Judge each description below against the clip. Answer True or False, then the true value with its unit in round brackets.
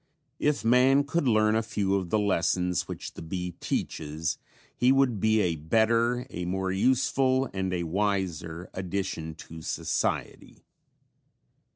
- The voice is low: True (100 Hz)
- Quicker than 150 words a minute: False (140 wpm)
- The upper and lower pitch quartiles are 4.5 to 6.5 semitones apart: True (4.8 semitones)